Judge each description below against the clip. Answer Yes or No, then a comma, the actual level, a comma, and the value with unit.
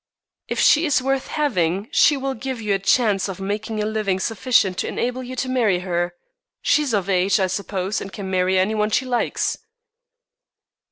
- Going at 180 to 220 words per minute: Yes, average, 190 wpm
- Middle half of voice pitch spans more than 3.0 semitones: Yes, average, 5.1 semitones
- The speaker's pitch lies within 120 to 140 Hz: No, high, 210 Hz